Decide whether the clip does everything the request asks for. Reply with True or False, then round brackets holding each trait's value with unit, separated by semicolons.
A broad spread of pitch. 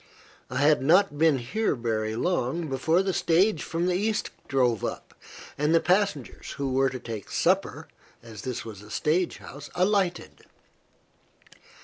True (6.4 semitones)